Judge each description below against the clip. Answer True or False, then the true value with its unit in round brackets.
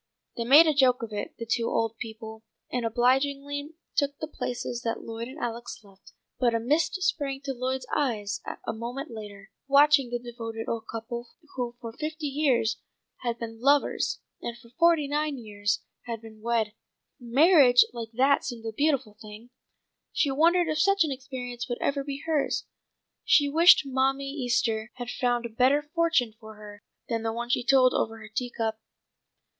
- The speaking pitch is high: True (245 Hz)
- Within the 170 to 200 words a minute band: True (180 wpm)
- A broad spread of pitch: False (3.8 semitones)